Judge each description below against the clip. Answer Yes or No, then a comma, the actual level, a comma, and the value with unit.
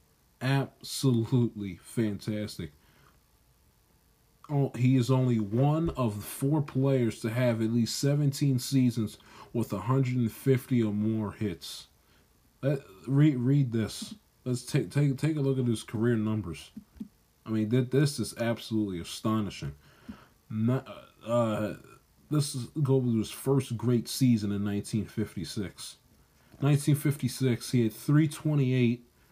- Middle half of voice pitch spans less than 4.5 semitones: Yes, average, 3.8 semitones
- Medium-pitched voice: No, low, 120 Hz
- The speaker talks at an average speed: No, slow, 115 wpm